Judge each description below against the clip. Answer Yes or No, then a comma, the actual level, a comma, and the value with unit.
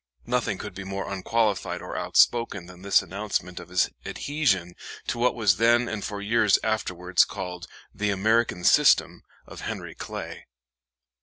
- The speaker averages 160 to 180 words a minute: No, average, 150 wpm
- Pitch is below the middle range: Yes, low, 100 Hz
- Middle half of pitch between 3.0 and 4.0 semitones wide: Yes, average, 3.7 semitones